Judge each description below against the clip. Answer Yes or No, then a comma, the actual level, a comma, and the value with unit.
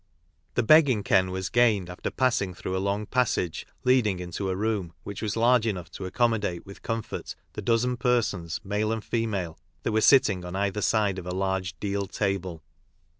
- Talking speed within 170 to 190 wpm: Yes, average, 180 wpm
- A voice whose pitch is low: Yes, low, 100 Hz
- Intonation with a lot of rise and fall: No, average, 3.5 semitones